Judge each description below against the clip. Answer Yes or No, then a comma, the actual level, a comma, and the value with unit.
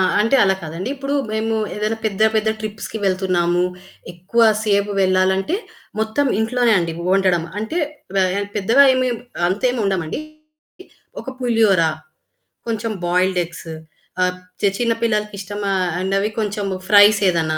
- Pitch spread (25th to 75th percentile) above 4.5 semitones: No, average, 3.0 semitones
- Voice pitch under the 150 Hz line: No, high, 205 Hz